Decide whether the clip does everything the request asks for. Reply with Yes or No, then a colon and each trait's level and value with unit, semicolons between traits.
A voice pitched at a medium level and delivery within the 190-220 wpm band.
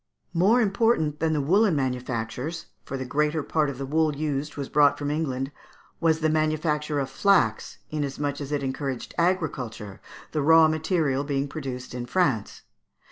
No: medium, 150 Hz; average, 165 wpm